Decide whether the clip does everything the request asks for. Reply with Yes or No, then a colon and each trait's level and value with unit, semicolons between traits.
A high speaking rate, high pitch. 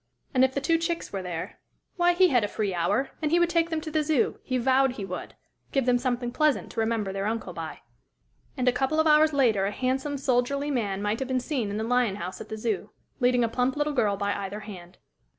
Yes: fast, 245 wpm; very high, 250 Hz